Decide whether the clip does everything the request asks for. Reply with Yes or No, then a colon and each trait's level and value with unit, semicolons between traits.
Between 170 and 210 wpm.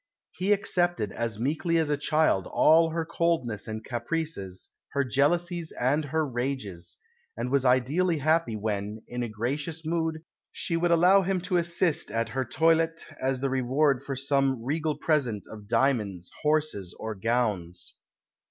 No: average, 150 wpm